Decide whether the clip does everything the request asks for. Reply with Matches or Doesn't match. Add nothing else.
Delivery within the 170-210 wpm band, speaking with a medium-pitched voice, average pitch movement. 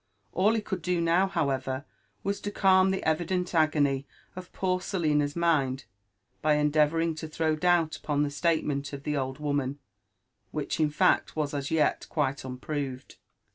Doesn't match